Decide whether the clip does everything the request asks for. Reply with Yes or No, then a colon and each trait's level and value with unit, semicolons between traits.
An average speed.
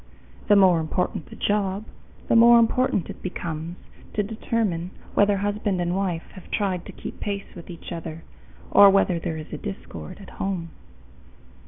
Yes: average, 160 wpm